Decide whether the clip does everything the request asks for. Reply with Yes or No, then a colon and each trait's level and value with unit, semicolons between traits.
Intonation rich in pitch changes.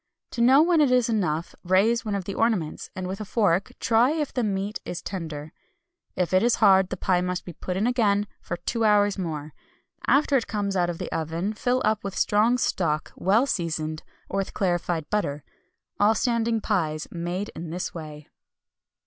No: average, 4.5 semitones